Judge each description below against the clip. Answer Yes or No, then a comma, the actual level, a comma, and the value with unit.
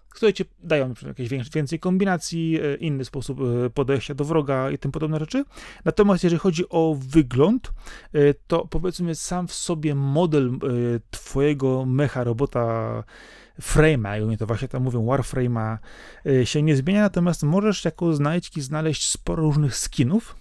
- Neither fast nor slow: Yes, average, 140 wpm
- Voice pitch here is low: No, medium, 150 Hz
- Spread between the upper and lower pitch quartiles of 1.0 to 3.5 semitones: No, average, 4.4 semitones